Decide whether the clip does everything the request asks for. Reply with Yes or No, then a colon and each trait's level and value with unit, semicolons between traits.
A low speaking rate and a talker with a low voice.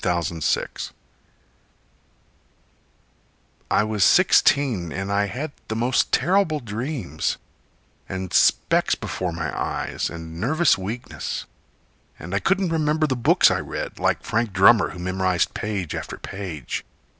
Yes: slow, 125 wpm; low, 105 Hz